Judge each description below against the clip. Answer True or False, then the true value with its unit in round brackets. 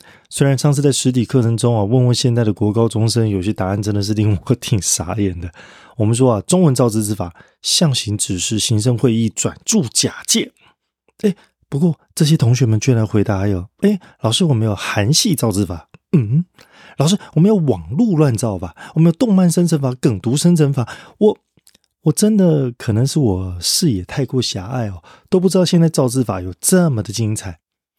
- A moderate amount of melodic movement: False (7.1 semitones)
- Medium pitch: False (125 Hz)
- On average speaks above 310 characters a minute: False (285 characters per minute)